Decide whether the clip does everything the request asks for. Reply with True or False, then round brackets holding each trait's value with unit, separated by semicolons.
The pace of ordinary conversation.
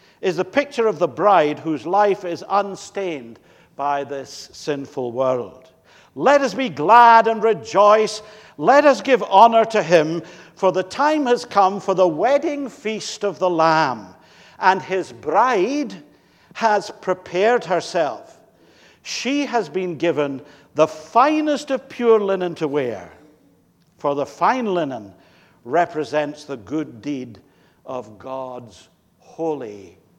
False (130 wpm)